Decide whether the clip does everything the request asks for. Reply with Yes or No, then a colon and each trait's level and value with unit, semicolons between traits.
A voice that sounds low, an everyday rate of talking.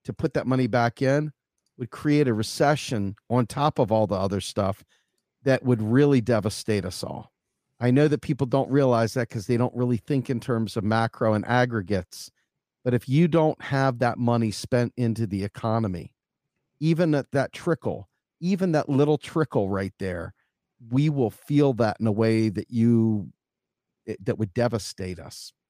Yes: low, 120 Hz; average, 175 wpm